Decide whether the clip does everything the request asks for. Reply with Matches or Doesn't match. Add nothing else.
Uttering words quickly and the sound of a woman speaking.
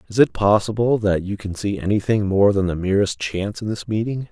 Doesn't match